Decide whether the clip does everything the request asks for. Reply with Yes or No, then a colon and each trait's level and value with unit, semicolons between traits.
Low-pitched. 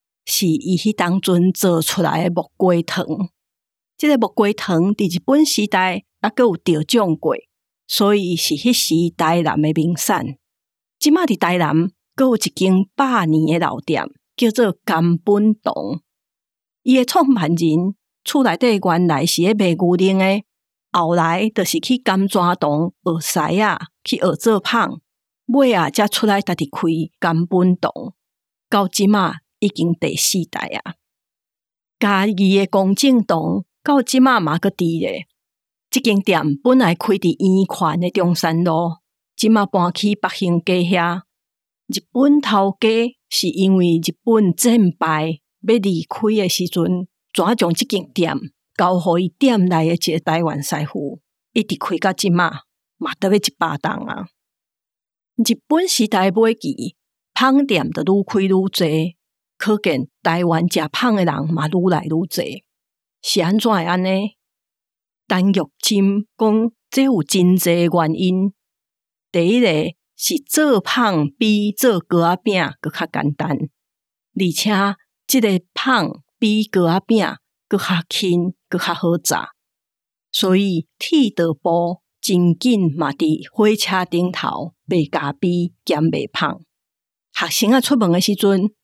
No: medium, 185 Hz